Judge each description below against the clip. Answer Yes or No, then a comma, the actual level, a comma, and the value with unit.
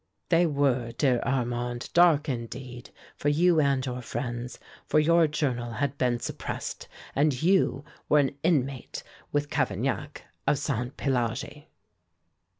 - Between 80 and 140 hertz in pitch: Yes, low, 135 Hz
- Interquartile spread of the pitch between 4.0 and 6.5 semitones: No, average, 3.4 semitones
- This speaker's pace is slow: Yes, slow, 130 wpm